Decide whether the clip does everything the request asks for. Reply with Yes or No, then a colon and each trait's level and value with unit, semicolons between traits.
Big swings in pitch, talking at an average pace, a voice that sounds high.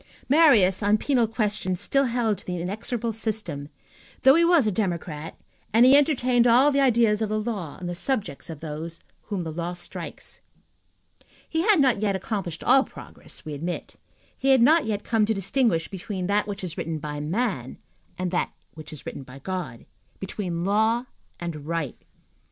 Yes: wide, 5.8 semitones; average, 180 wpm; high, 205 Hz